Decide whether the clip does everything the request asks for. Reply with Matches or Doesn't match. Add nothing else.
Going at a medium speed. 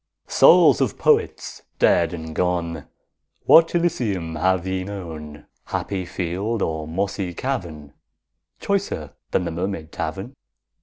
Doesn't match